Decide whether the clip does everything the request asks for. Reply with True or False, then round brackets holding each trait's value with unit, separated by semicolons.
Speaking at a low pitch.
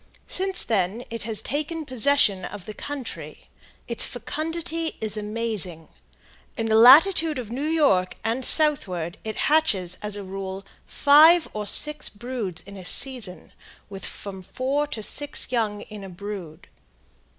False (225 Hz)